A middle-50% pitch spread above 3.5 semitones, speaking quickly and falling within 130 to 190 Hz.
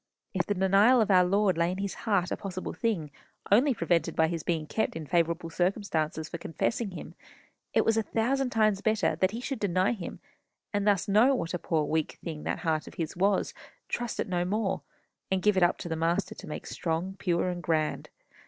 Yes: average, 3.9 semitones; fast, 225 wpm; medium, 185 Hz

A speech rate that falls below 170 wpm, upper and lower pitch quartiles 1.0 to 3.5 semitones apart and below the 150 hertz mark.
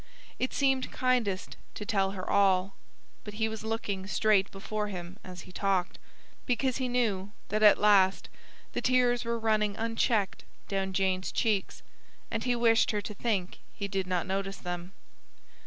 No: average, 160 wpm; average, 2.9 semitones; high, 205 Hz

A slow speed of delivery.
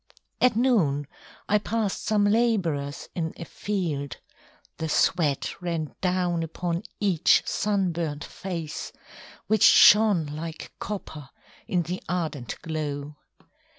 Yes: slow, 110 wpm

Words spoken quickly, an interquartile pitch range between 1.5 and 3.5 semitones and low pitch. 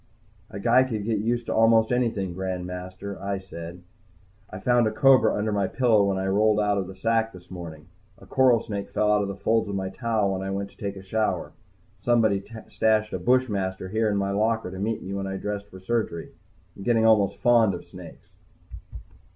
Yes: fast, 210 wpm; average, 2.8 semitones; low, 100 Hz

